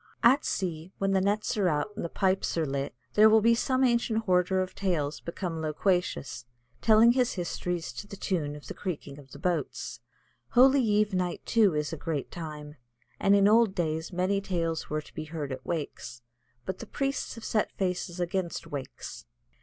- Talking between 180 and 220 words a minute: Yes, average, 185 wpm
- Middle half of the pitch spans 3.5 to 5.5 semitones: Yes, average, 4.8 semitones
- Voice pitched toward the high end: No, medium, 180 Hz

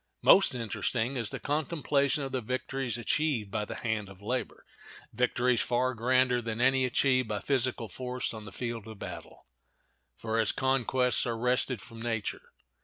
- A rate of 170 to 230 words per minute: No, average, 160 wpm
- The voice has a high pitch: No, low, 125 Hz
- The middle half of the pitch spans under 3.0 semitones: Yes, narrow, 2.4 semitones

